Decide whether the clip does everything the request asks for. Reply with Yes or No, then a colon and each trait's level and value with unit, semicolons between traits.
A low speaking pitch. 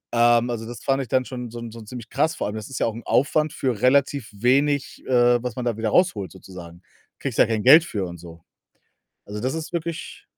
Yes: low, 120 Hz